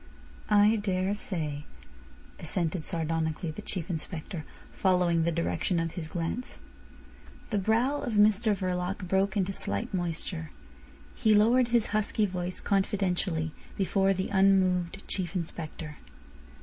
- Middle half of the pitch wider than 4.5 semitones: No, average, 3.4 semitones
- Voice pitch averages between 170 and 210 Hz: Yes, medium, 185 Hz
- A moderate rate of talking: No, slow, 120 wpm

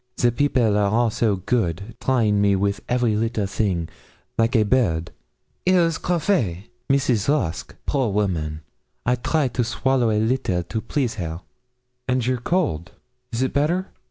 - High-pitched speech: No, low, 115 Hz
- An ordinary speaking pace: Yes, average, 160 wpm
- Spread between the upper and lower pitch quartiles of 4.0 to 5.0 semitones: Yes, average, 4.7 semitones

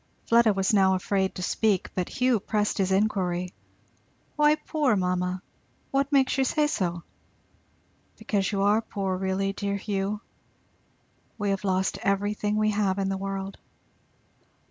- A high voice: Yes, high, 200 Hz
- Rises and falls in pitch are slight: Yes, narrow, 2.1 semitones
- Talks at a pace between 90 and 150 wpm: Yes, average, 145 wpm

